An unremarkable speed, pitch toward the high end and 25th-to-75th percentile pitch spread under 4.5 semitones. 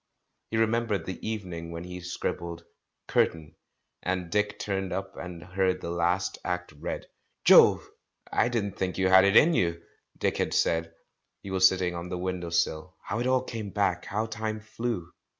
No: average, 185 wpm; very low, 95 Hz; average, 3.2 semitones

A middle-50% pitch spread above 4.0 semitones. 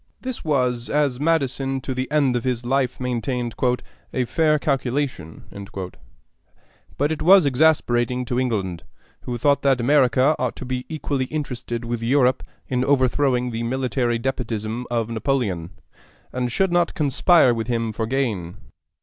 No: average, 2.9 semitones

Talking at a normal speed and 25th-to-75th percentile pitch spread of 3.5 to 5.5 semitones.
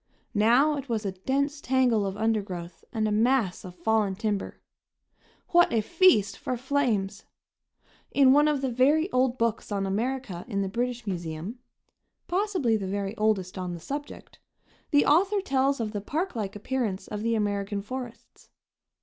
Yes: average, 160 wpm; average, 5.1 semitones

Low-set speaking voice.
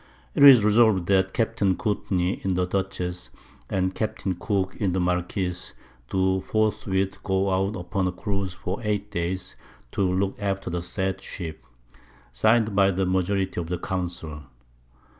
Yes: very low, 95 Hz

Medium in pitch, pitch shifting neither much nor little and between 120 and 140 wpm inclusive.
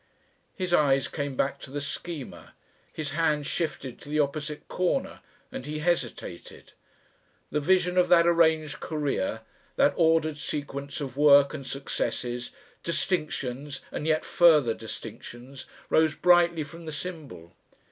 Yes: medium, 150 Hz; average, 3.0 semitones; slow, 135 wpm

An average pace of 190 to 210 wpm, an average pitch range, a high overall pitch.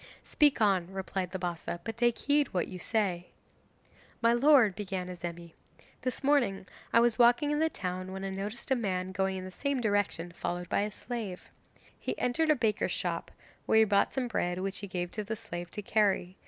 Yes: average, 200 wpm; average, 4.6 semitones; high, 200 Hz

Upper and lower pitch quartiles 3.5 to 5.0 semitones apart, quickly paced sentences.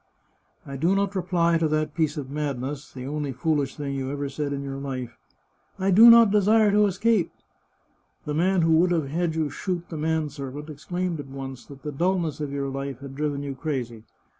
Yes: average, 4.1 semitones; fast, 215 wpm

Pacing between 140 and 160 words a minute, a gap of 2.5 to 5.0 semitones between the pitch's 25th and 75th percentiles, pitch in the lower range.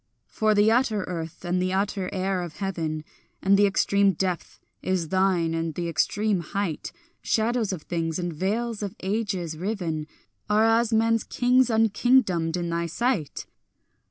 No: average, 155 wpm; average, 4.3 semitones; high, 190 Hz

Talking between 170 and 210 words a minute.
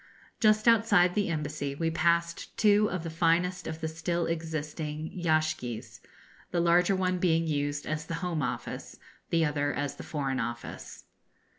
No: average, 155 wpm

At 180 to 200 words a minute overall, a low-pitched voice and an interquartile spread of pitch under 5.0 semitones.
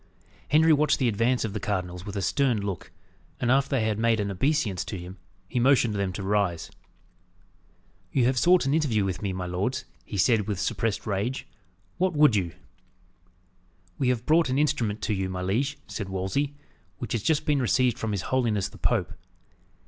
No: average, 190 wpm; low, 110 Hz; wide, 5.5 semitones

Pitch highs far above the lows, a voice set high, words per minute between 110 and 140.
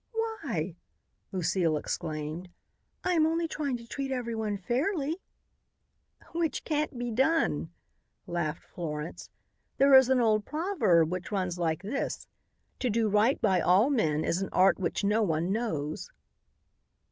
Yes: wide, 7.9 semitones; high, 215 Hz; slow, 135 wpm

